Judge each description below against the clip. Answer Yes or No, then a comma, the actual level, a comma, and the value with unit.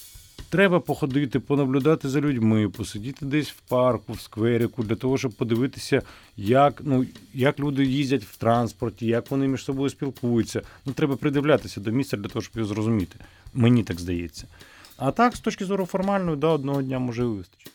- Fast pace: Yes, fast, 175 wpm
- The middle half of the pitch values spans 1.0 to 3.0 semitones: No, average, 4.2 semitones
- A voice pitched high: No, low, 125 Hz